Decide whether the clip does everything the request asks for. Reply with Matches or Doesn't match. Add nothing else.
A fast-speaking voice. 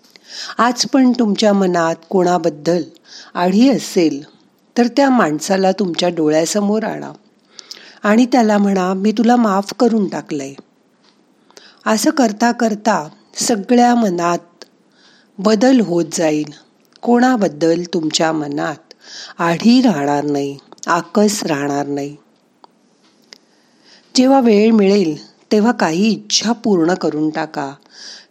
Doesn't match